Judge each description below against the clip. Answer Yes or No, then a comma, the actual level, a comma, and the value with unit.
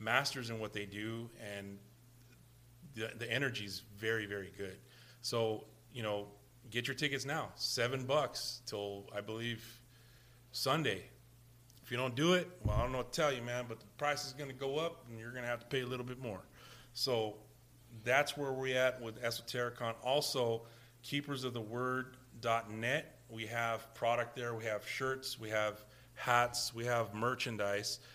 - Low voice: Yes, low, 120 Hz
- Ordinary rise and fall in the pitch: No, narrow, 2.2 semitones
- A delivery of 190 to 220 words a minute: No, average, 170 wpm